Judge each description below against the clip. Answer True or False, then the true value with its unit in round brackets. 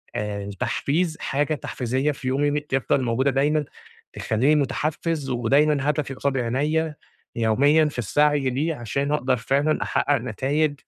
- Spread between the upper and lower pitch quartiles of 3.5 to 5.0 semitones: False (2.7 semitones)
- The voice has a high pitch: False (140 Hz)